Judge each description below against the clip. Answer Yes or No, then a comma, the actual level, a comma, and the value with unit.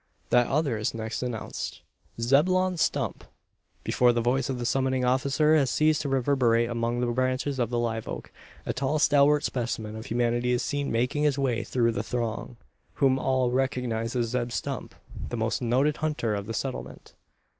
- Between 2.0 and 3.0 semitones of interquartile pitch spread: Yes, average, 2.7 semitones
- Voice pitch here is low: Yes, low, 125 Hz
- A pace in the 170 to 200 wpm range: Yes, average, 175 wpm